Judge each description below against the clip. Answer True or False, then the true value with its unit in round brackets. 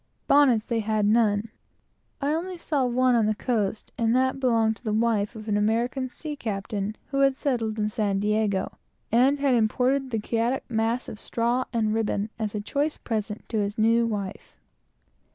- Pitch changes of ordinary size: True (3.2 semitones)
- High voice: True (225 Hz)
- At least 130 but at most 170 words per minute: False (180 wpm)